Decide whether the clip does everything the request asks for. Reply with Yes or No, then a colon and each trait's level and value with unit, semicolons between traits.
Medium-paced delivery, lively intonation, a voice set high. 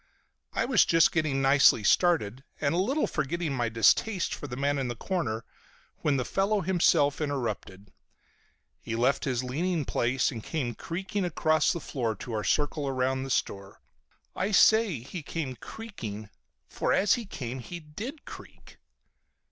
No: average, 160 wpm; wide, 6.0 semitones; medium, 145 Hz